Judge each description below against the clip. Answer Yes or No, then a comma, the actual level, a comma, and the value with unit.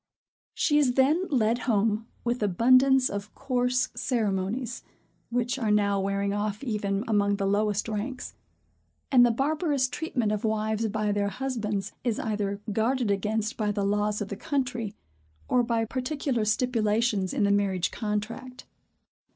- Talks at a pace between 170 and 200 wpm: No, average, 145 wpm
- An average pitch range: Yes, average, 3.5 semitones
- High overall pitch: Yes, high, 220 Hz